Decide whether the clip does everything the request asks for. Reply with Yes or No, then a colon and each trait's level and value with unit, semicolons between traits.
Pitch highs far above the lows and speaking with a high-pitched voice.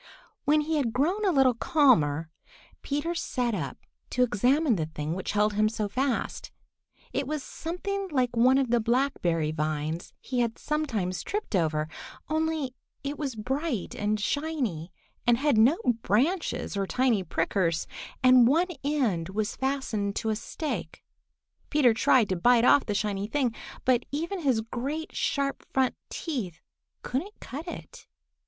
Yes: wide, 5.9 semitones; very high, 250 Hz